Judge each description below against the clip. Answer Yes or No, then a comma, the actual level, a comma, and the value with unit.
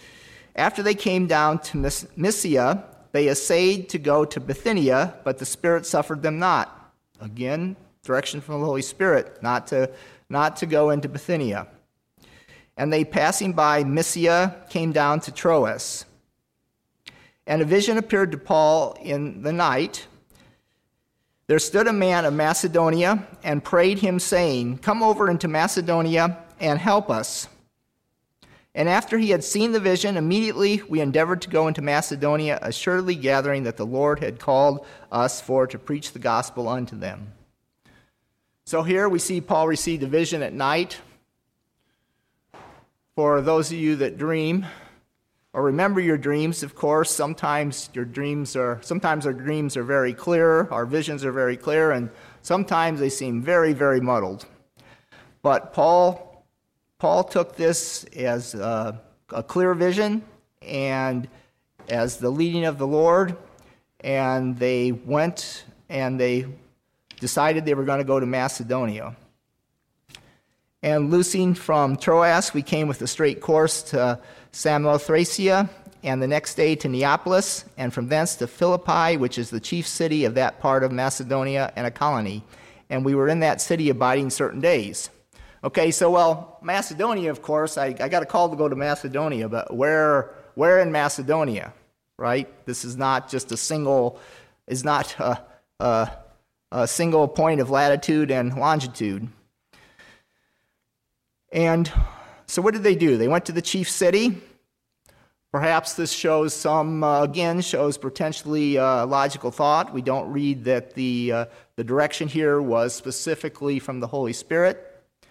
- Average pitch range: Yes, average, 4.5 semitones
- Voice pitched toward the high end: No, medium, 150 Hz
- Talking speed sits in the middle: Yes, average, 150 wpm